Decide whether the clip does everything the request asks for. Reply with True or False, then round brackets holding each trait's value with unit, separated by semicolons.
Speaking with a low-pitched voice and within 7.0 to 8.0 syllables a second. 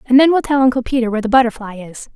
False (245 Hz; 7.4 syllables/s)